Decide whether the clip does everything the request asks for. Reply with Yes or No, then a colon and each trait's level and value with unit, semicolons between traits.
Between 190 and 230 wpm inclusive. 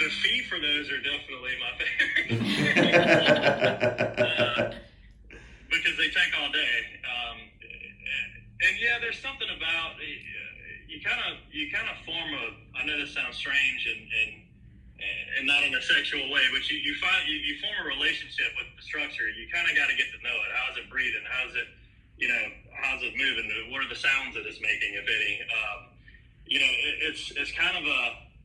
Yes: average, 200 wpm